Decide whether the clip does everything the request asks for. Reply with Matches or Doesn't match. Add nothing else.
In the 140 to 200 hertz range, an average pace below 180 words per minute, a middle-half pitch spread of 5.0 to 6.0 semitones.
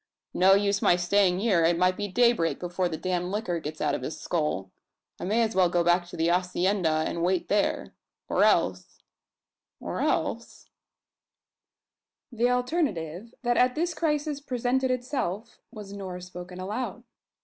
Matches